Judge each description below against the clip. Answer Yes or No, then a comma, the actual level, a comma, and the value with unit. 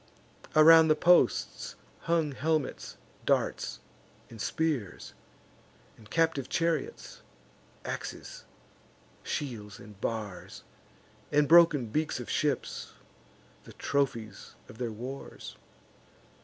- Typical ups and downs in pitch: No, wide, 6.1 semitones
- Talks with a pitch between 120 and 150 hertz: Yes, medium, 140 Hz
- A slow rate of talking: Yes, slow, 90 wpm